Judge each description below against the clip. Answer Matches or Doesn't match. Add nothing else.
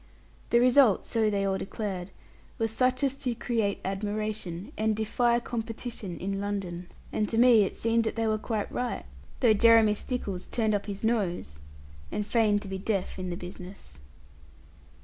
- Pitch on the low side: Doesn't match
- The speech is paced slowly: Doesn't match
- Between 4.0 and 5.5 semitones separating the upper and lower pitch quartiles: Doesn't match